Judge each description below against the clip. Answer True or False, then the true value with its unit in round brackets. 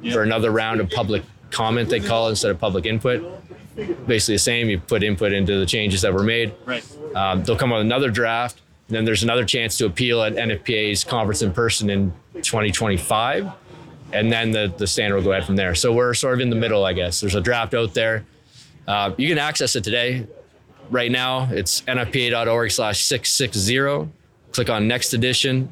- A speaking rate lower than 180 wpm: False (195 wpm)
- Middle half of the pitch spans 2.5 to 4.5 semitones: True (3.3 semitones)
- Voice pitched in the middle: False (115 Hz)